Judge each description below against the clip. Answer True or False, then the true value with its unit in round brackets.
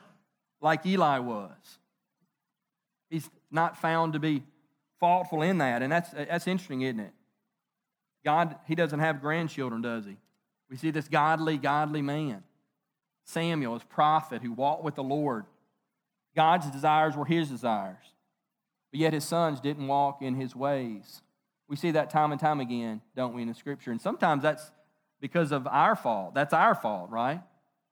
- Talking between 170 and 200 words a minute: False (160 wpm)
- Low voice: False (150 Hz)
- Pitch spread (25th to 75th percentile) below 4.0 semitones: True (2.7 semitones)